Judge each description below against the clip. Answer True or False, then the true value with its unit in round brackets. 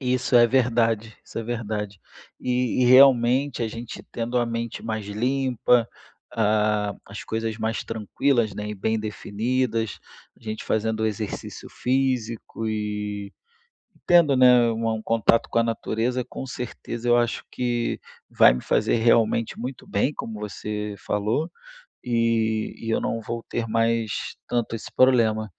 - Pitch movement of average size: False (2.0 semitones)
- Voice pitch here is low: True (115 Hz)